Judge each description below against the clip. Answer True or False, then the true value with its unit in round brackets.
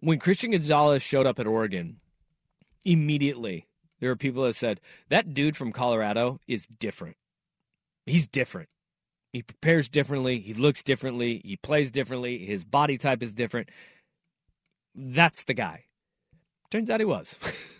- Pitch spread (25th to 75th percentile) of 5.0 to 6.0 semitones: False (4.5 semitones)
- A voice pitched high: False (140 Hz)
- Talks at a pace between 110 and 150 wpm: True (140 wpm)